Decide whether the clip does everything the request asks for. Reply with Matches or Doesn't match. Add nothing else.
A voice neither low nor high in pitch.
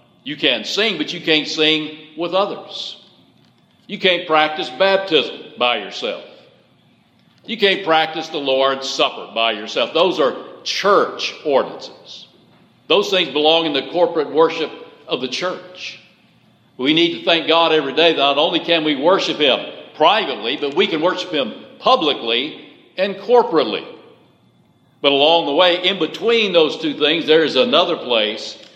Matches